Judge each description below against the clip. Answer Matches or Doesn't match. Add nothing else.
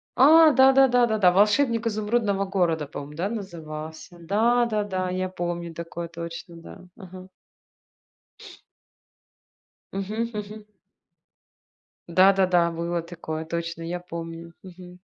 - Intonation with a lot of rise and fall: Doesn't match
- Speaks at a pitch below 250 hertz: Matches